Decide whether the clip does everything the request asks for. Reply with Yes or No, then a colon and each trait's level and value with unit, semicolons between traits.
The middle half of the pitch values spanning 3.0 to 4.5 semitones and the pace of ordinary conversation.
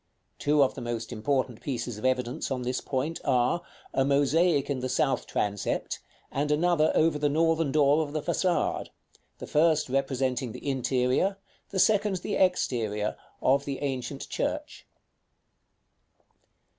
Yes: average, 3.5 semitones; average, 145 wpm